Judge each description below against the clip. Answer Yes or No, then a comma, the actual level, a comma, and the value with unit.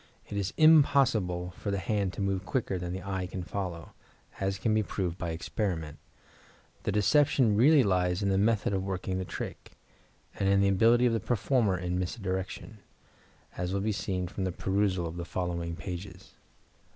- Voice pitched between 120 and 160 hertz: No, very low, 95 Hz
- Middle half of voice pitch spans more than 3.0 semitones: No, average, 2.7 semitones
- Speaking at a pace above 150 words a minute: Yes, average, 180 wpm